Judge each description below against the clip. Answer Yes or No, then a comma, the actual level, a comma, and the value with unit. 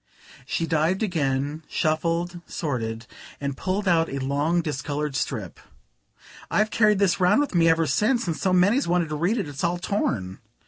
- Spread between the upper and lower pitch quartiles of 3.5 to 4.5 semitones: Yes, average, 4.2 semitones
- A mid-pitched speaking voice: Yes, medium, 165 Hz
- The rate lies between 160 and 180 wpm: Yes, average, 170 wpm